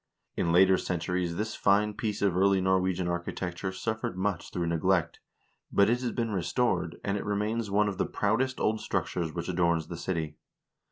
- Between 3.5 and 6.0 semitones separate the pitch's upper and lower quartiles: No, average, 3.1 semitones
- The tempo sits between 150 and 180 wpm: Yes, average, 175 wpm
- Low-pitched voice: Yes, very low, 95 Hz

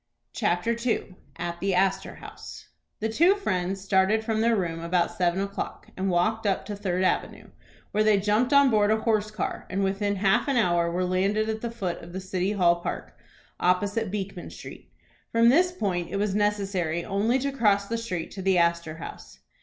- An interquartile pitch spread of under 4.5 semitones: Yes, average, 3.3 semitones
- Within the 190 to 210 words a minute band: Yes, average, 195 wpm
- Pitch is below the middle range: No, high, 200 Hz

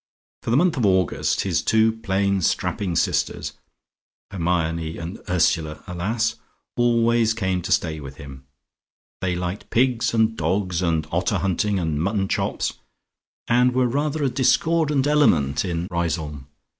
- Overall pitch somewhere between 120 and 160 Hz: No, very low, 95 Hz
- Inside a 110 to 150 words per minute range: Yes, average, 140 wpm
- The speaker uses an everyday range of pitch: No, wide, 5.8 semitones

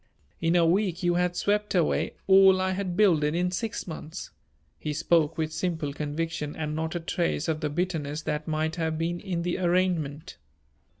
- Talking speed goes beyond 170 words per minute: Yes, average, 180 wpm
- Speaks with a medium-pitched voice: Yes, medium, 165 Hz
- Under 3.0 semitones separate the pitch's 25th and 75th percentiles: Yes, narrow, 2.6 semitones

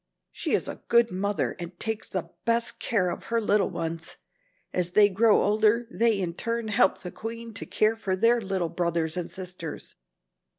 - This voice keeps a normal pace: Yes, average, 185 wpm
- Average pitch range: Yes, average, 4.1 semitones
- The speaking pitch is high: Yes, high, 200 Hz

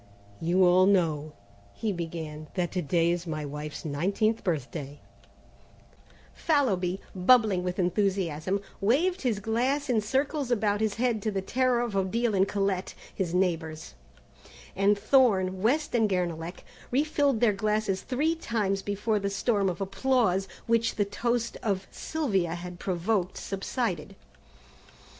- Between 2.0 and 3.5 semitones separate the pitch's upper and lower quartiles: No, average, 4.4 semitones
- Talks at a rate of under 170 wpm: Yes, average, 140 wpm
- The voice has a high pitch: Yes, high, 195 Hz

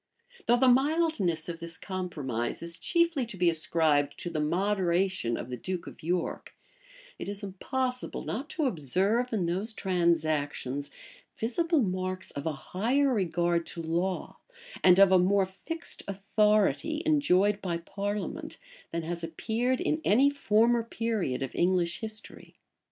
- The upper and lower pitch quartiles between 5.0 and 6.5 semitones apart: Yes, average, 5.3 semitones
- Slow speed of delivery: No, average, 145 wpm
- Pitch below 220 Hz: Yes, high, 190 Hz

